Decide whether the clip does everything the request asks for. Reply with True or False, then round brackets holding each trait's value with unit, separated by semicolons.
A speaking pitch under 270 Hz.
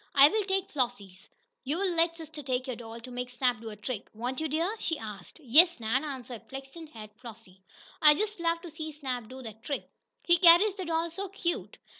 False (275 Hz)